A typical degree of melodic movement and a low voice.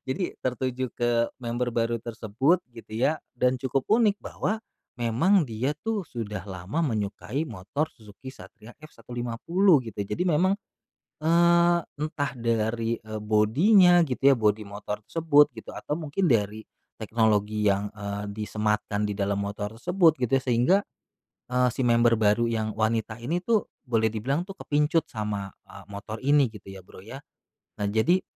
No: wide, 5.7 semitones; low, 120 Hz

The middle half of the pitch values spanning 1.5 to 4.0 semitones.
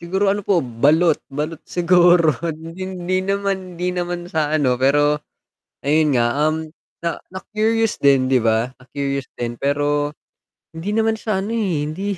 No: average, 4.5 semitones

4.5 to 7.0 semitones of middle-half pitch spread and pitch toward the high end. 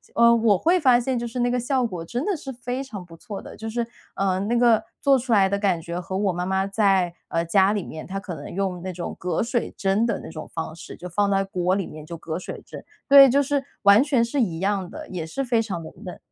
Yes: average, 4.8 semitones; high, 200 Hz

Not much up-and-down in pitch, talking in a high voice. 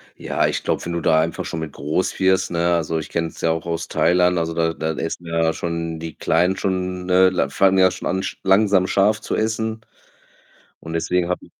No: narrow, 2.2 semitones; very low, 85 Hz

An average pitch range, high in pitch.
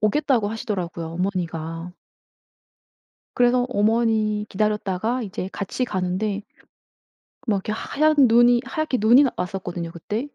Yes: average, 4.5 semitones; high, 210 Hz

